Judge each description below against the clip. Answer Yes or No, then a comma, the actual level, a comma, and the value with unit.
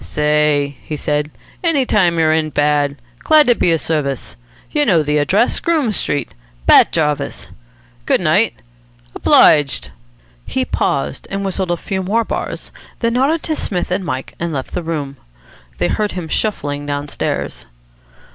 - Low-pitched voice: No, medium, 160 Hz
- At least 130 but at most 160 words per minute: Yes, average, 155 wpm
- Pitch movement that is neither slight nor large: No, wide, 5.8 semitones